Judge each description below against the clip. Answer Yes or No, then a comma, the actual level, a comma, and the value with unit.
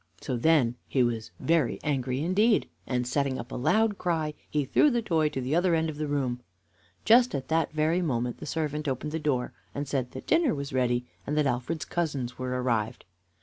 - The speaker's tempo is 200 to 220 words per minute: Yes, fast, 205 wpm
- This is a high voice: No, medium, 145 Hz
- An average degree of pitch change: Yes, average, 4.3 semitones